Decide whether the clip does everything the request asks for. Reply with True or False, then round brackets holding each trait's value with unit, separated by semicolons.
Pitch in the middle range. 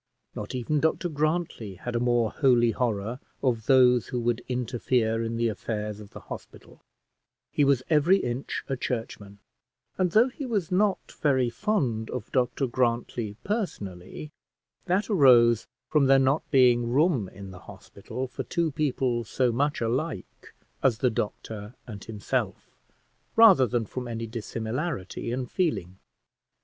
False (125 Hz)